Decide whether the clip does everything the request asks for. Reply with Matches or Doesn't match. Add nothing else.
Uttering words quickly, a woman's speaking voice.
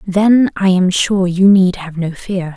Matches